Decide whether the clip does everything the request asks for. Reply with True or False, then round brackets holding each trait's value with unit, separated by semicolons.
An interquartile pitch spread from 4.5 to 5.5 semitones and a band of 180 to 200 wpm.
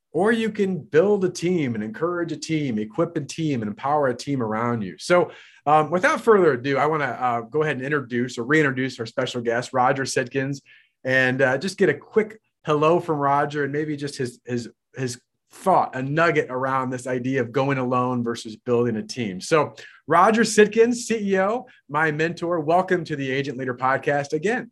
True (5.1 semitones; 195 wpm)